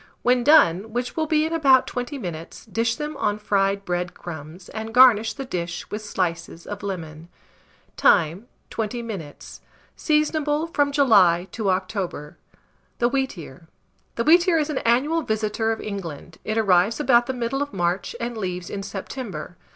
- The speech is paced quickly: No, average, 160 wpm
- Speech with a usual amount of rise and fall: No, wide, 6.5 semitones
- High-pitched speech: Yes, high, 220 Hz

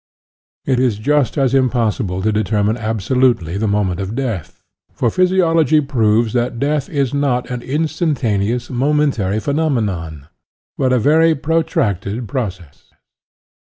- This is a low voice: Yes, low, 120 Hz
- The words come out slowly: Yes, slow, 130 wpm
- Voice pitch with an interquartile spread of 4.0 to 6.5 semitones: Yes, average, 5.3 semitones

